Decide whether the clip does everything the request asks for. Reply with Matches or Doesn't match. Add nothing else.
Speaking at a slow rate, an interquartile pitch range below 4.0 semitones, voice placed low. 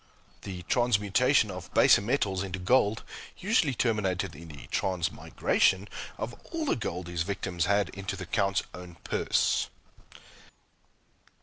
Matches